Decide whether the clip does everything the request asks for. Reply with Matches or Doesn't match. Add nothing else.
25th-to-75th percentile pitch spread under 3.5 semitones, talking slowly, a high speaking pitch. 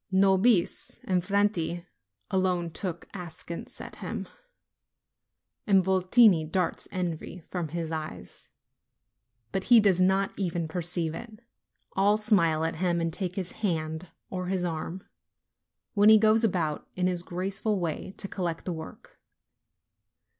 Doesn't match